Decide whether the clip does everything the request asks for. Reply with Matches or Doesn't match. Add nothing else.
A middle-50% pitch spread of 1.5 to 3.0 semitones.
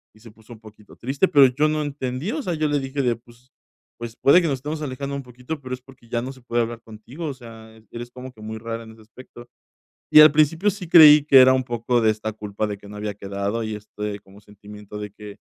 Doesn't match